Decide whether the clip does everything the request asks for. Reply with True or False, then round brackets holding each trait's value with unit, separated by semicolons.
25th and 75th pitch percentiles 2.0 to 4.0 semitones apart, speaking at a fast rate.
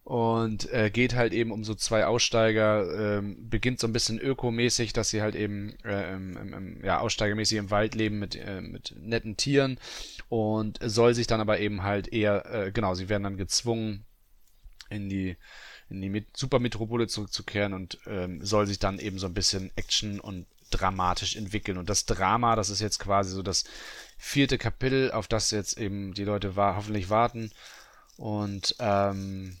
False (2.4 semitones; 175 wpm)